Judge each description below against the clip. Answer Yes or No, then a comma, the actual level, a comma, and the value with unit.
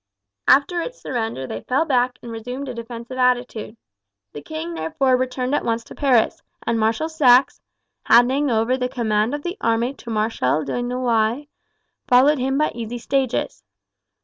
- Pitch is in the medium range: No, high, 245 Hz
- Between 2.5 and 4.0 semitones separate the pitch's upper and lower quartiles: Yes, average, 2.8 semitones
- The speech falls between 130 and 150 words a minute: No, average, 160 wpm